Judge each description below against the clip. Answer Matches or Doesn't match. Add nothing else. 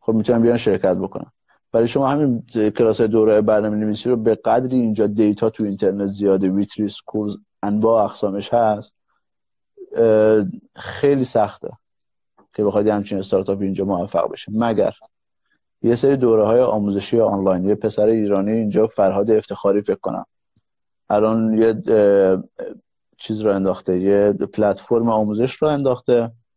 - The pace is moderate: Matches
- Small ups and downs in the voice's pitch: Matches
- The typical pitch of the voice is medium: Doesn't match